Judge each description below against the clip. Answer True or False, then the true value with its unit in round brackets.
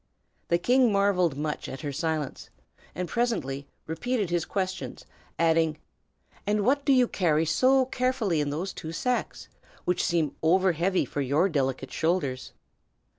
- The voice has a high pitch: False (175 Hz)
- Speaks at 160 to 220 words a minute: False (145 wpm)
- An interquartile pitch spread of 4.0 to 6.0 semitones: True (5.3 semitones)